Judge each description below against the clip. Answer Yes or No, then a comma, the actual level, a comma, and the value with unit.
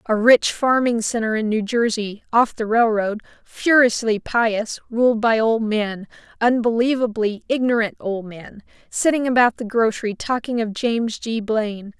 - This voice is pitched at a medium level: No, high, 225 Hz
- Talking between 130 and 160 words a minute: Yes, average, 145 wpm